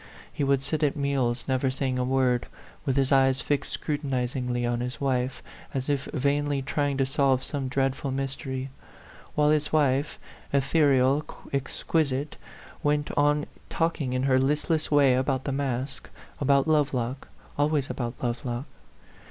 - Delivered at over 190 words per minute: No, average, 150 wpm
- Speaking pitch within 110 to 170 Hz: Yes, low, 135 Hz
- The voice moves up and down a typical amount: No, narrow, 2.0 semitones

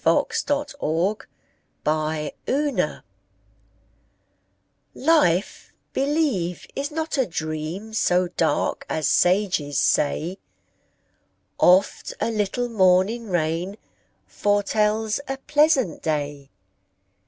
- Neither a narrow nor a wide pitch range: No, wide, 8.1 semitones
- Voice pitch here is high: Yes, high, 195 Hz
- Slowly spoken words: Yes, slow, 80 wpm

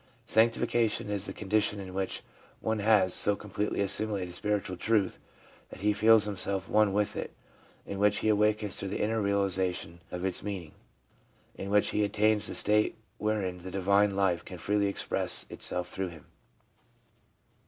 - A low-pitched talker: Yes, low, 100 Hz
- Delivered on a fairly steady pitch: Yes, narrow, 1.9 semitones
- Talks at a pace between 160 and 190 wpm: Yes, average, 165 wpm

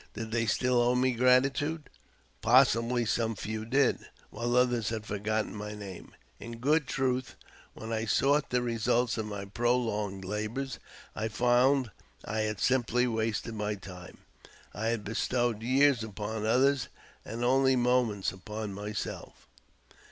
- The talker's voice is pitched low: Yes, low, 115 Hz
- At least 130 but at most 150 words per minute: Yes, slow, 135 wpm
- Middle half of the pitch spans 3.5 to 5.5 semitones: No, average, 2.8 semitones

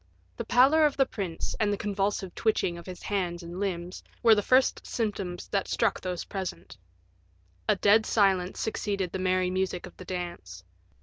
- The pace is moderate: Yes, average, 175 wpm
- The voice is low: No, high, 190 Hz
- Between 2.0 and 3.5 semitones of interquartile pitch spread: Yes, average, 2.7 semitones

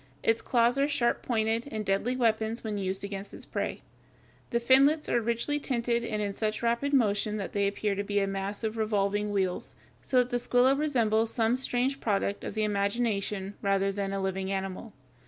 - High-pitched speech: Yes, high, 220 Hz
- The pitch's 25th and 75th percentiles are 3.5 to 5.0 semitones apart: No, average, 3.1 semitones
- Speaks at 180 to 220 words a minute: Yes, average, 190 wpm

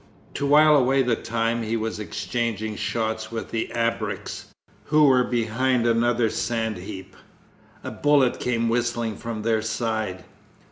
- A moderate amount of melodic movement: No, narrow, 1.8 semitones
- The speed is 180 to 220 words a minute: No, average, 140 wpm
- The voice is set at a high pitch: No, low, 115 Hz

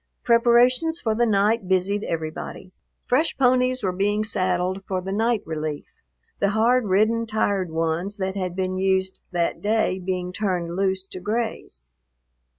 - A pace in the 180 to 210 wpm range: No, average, 150 wpm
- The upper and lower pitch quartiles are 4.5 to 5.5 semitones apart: No, average, 3.5 semitones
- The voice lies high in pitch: Yes, high, 195 Hz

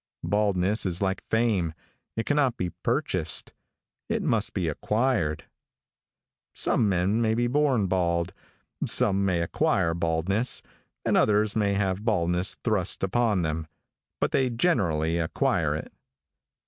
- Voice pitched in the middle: No, low, 100 Hz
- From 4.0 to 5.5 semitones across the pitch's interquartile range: Yes, average, 4.5 semitones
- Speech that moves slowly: Yes, slow, 125 wpm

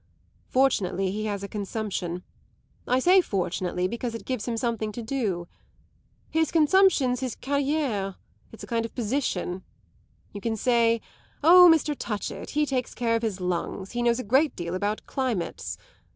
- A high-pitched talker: Yes, high, 230 Hz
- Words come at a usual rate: Yes, average, 160 wpm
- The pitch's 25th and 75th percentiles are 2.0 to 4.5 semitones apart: No, average, 5.1 semitones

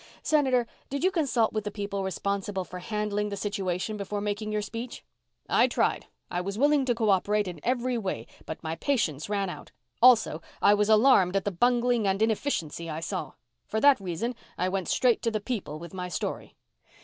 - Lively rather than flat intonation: No, average, 3.9 semitones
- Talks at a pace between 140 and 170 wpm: No, average, 195 wpm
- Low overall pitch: No, high, 210 Hz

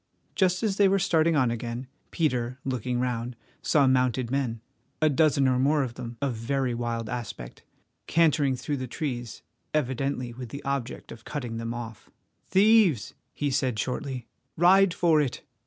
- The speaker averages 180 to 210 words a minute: No, average, 155 wpm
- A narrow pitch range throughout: No, average, 4.0 semitones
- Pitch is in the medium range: No, low, 130 Hz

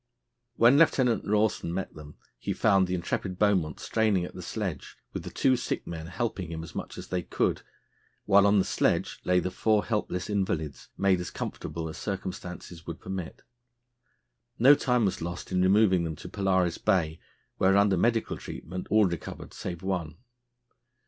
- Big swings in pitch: No, average, 3.2 semitones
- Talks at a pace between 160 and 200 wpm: Yes, average, 170 wpm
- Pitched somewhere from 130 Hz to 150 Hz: No, very low, 95 Hz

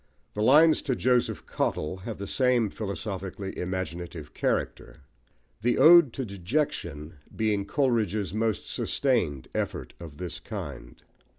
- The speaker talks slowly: Yes, slow, 120 wpm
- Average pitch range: No, wide, 5.9 semitones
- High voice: No, low, 105 Hz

